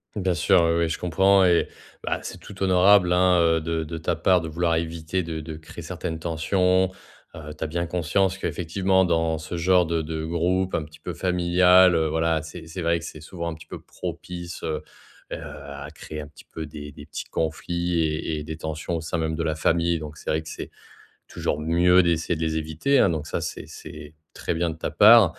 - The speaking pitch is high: No, very low, 85 Hz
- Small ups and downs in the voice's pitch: Yes, narrow, 2.2 semitones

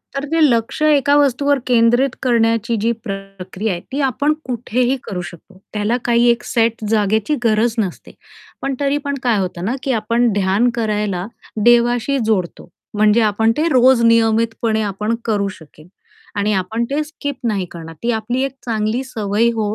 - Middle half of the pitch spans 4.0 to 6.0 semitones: No, average, 3.0 semitones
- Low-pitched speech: No, high, 230 Hz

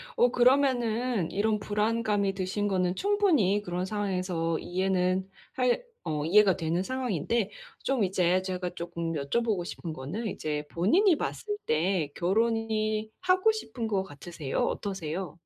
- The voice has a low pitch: No, high, 195 Hz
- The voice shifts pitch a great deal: No, average, 4.7 semitones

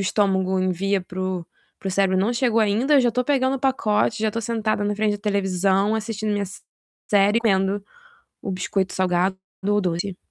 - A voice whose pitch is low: No, high, 200 Hz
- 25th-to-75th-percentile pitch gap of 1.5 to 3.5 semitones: Yes, narrow, 2.5 semitones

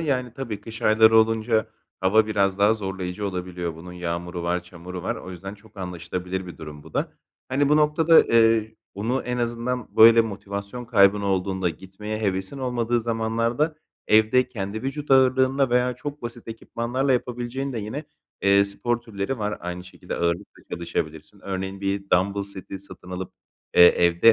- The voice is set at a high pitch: No, low, 105 Hz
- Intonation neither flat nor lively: Yes, average, 4.2 semitones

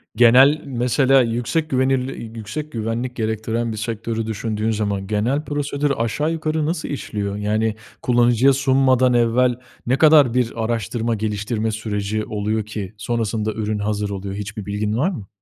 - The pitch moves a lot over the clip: No, average, 3.4 semitones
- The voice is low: Yes, low, 115 Hz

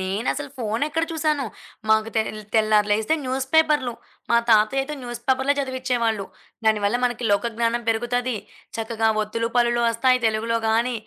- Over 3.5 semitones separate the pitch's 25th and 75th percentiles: No, average, 2.8 semitones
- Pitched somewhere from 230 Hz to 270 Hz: Yes, high, 235 Hz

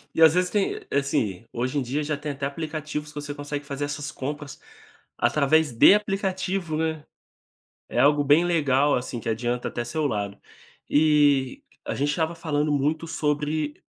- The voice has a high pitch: No, medium, 145 Hz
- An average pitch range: No, narrow, 2.2 semitones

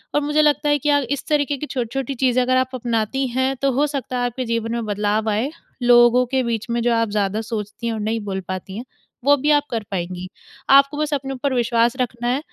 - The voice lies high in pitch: Yes, high, 245 Hz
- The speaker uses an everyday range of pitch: Yes, average, 3.3 semitones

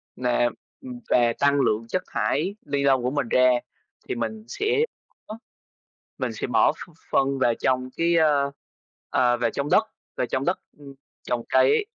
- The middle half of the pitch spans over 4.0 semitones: No, average, 3.3 semitones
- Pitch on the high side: No, low, 135 Hz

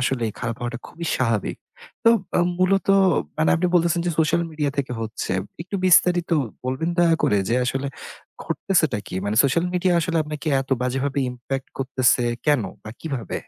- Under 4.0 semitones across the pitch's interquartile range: No, average, 5.3 semitones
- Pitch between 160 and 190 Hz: No, medium, 140 Hz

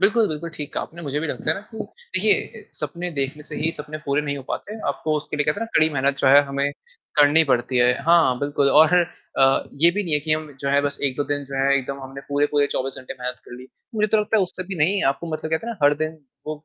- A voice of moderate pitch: Yes, medium, 150 Hz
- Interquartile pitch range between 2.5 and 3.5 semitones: Yes, average, 3.2 semitones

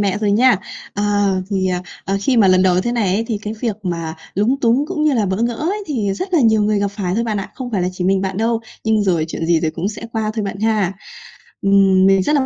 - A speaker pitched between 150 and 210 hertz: Yes, high, 205 Hz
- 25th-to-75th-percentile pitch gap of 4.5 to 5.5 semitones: No, average, 3.4 semitones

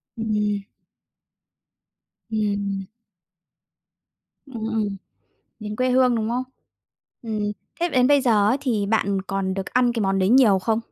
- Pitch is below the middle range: No, high, 215 Hz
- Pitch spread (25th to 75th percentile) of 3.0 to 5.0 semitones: Yes, average, 3.3 semitones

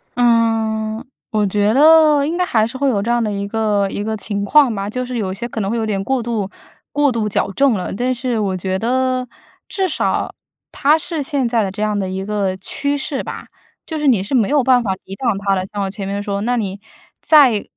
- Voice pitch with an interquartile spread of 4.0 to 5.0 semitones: Yes, average, 4.4 semitones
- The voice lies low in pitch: No, high, 225 Hz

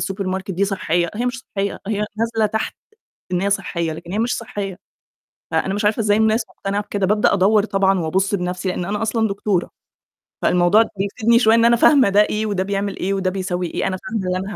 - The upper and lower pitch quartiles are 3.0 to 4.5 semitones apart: No, narrow, 2.5 semitones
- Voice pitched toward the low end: No, high, 200 Hz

